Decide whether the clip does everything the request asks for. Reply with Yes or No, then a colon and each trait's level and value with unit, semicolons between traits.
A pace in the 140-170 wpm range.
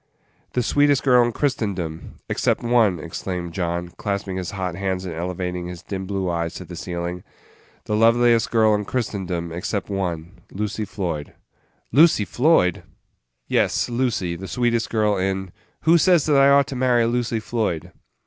Yes: average, 160 wpm